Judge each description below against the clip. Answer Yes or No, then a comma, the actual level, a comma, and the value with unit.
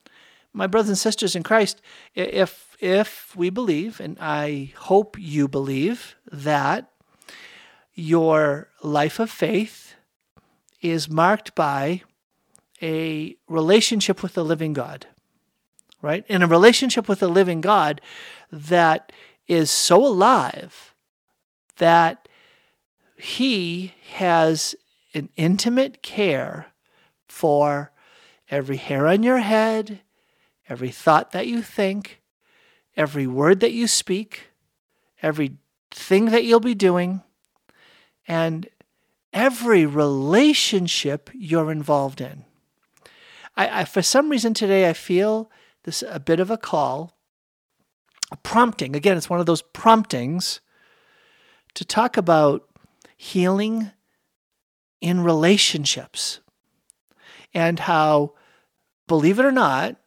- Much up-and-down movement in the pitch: Yes, wide, 6.1 semitones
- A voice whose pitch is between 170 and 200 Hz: Yes, medium, 185 Hz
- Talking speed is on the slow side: Yes, slow, 110 wpm